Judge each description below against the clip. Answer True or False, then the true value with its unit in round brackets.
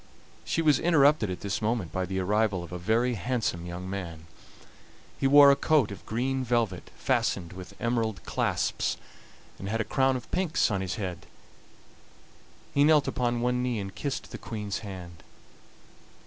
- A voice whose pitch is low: True (110 Hz)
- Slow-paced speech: False (165 wpm)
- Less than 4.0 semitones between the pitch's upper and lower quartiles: False (5.5 semitones)